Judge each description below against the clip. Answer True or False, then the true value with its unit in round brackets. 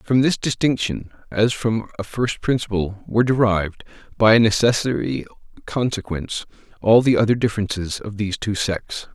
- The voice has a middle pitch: False (110 Hz)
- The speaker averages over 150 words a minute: False (145 wpm)